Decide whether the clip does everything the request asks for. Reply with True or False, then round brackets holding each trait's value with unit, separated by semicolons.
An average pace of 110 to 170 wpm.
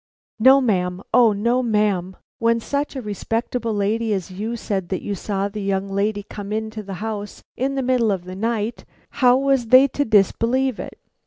False (185 wpm)